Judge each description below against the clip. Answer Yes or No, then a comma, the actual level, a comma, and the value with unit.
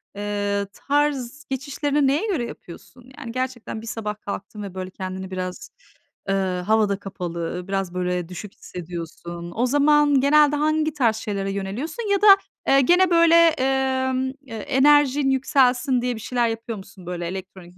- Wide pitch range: Yes, wide, 6.6 semitones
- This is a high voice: Yes, high, 240 Hz